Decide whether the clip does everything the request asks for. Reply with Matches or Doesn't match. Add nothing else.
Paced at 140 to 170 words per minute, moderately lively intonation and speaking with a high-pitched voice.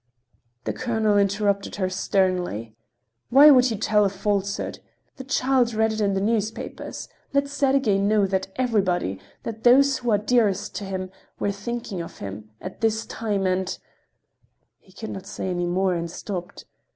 Matches